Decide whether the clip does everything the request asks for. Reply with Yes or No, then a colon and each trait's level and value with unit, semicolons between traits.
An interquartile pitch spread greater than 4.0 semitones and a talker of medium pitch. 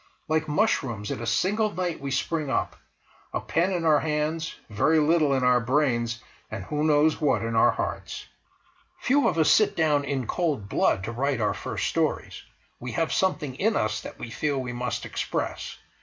Yes: average, 4.9 semitones; medium, 145 Hz